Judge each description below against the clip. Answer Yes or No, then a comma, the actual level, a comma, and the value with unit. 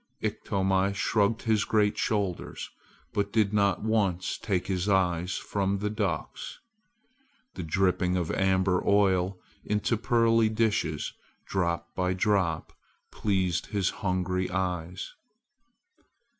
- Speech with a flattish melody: Yes, narrow, 2.3 semitones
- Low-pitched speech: Yes, very low, 95 Hz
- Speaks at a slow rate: Yes, slow, 110 wpm